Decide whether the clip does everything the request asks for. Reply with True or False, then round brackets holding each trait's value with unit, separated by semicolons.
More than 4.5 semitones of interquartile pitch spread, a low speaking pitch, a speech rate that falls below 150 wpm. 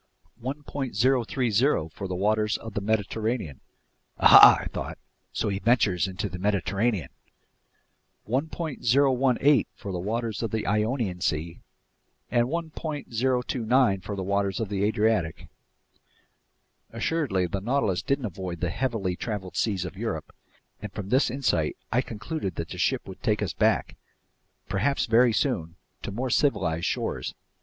True (4.9 semitones; 110 Hz; 135 wpm)